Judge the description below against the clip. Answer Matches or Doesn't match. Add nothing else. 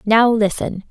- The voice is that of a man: Doesn't match